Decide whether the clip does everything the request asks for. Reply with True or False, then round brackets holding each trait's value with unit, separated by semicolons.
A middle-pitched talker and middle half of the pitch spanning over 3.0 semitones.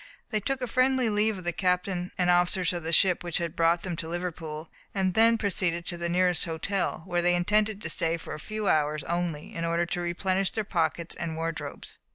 False (175 Hz; 2.7 semitones)